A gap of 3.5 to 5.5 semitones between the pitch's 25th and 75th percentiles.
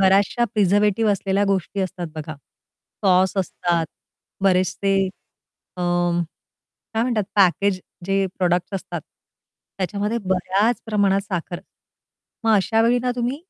No: narrow, 2.4 semitones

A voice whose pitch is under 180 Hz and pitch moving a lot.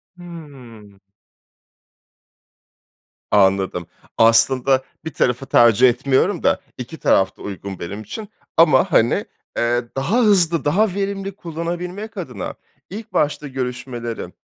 Yes: low, 135 Hz; wide, 7.1 semitones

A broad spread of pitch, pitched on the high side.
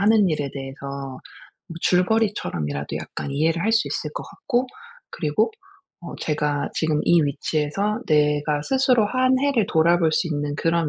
No: wide, 6.4 semitones; medium, 165 Hz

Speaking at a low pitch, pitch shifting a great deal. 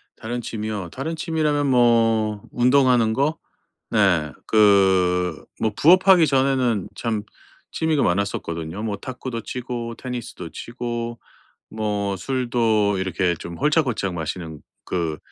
No: low, 115 Hz; average, 4.5 semitones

